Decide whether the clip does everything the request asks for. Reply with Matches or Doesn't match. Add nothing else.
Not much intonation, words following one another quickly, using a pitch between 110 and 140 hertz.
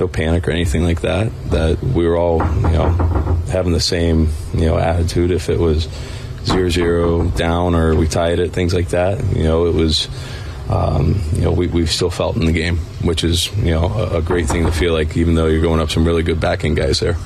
Doesn't match